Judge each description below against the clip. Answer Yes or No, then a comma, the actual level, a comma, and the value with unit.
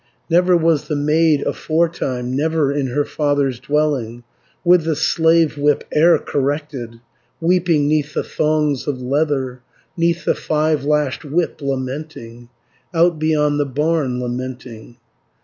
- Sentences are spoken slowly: Yes, slow, 130 wpm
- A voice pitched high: No, medium, 150 Hz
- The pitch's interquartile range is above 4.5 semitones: No, average, 3.2 semitones